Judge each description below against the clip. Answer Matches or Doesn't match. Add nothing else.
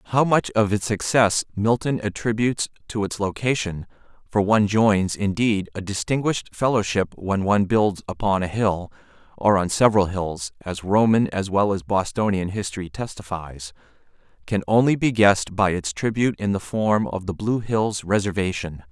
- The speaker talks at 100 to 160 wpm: Matches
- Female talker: Doesn't match